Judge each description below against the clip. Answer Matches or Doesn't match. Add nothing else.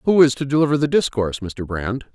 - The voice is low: Matches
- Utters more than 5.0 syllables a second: Matches